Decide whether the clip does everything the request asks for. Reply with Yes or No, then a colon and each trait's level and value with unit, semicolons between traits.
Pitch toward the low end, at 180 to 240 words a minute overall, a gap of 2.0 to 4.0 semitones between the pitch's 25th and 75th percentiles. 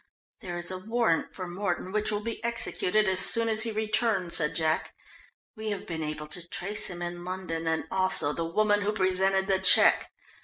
No: high, 190 Hz; average, 195 wpm; average, 3.5 semitones